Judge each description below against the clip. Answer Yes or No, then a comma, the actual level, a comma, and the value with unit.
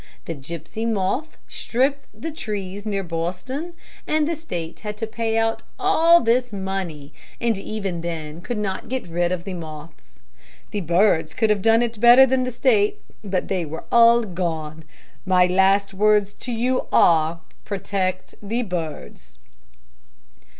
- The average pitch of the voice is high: Yes, high, 200 Hz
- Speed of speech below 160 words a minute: Yes, average, 150 wpm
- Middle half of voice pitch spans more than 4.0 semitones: Yes, average, 5.2 semitones